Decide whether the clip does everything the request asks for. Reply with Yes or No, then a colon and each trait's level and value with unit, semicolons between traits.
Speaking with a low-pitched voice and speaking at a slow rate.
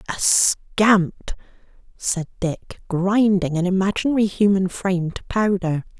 No: high, 190 Hz; slow, 110 wpm